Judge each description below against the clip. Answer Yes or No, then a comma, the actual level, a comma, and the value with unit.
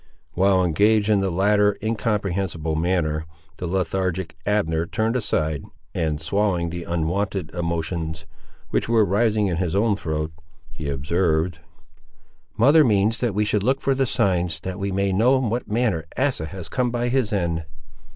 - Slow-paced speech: No, average, 160 wpm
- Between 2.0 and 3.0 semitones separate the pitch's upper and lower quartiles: No, average, 4.2 semitones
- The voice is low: Yes, very low, 95 Hz